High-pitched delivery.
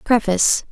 Yes: high, 215 Hz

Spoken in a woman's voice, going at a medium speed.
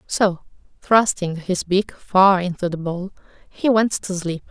Yes: female; average, 160 wpm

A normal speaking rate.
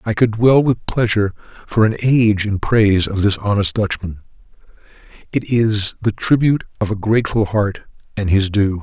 Yes: average, 170 wpm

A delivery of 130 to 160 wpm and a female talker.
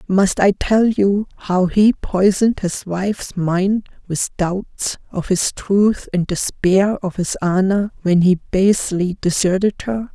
Yes: average, 150 wpm; female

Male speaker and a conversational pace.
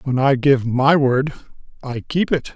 Yes: male; average, 190 wpm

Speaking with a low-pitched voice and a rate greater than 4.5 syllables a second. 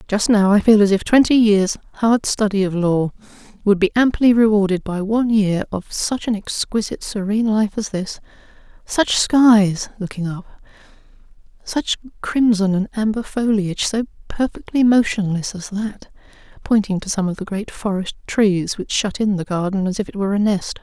No: high, 205 Hz; 4.9 syllables/s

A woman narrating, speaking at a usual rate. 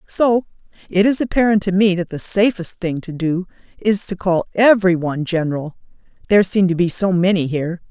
Yes: female; average, 175 wpm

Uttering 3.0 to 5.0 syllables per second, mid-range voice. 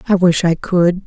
Yes: 4.5 syllables/s; medium, 175 Hz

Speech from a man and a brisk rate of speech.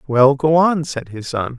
Yes: male; fast, 225 wpm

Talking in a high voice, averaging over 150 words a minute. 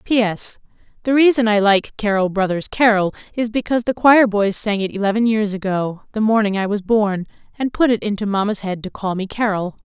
Yes: high, 210 Hz; average, 200 wpm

